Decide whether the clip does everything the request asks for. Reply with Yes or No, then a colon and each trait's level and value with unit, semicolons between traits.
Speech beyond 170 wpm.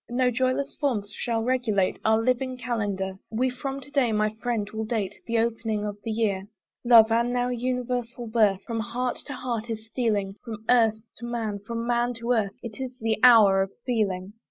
Yes: average, 190 wpm